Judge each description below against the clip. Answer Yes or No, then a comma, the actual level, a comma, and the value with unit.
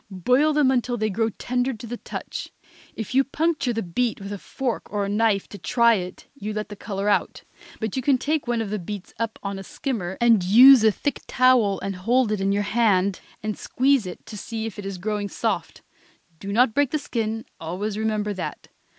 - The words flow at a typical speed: No, fast, 215 wpm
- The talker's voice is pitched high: Yes, high, 220 Hz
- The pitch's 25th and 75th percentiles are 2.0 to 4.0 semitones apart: Yes, average, 3.7 semitones